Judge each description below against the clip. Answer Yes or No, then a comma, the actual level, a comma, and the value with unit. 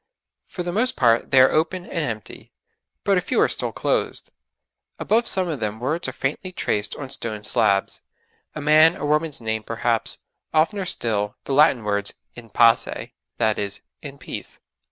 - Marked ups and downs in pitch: Yes, wide, 6.7 semitones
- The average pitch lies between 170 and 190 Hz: No, low, 135 Hz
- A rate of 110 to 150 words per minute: No, average, 175 wpm